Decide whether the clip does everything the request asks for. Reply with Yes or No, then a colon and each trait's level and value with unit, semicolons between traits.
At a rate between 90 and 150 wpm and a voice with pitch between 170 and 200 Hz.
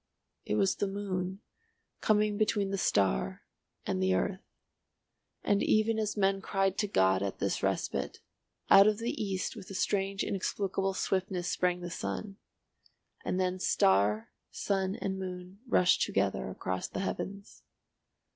Yes: average, 145 wpm; high, 190 Hz